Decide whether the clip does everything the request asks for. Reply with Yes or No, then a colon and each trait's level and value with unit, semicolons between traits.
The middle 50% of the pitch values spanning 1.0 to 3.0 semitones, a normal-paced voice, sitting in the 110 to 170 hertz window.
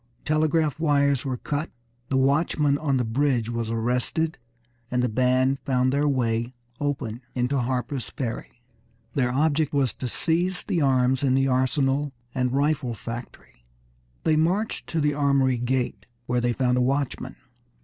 Yes: average, 2.7 semitones; average, 150 wpm; low, 135 Hz